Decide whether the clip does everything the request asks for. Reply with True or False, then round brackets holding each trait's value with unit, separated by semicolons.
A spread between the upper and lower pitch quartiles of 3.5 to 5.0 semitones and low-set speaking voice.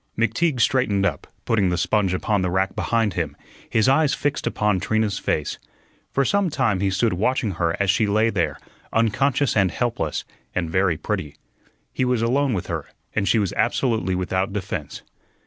True (4.5 semitones; 105 Hz)